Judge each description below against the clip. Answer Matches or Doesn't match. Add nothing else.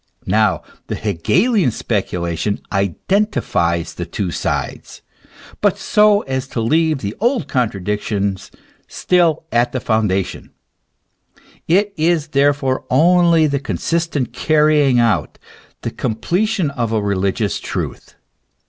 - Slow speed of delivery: Matches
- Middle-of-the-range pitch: Doesn't match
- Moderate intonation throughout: Doesn't match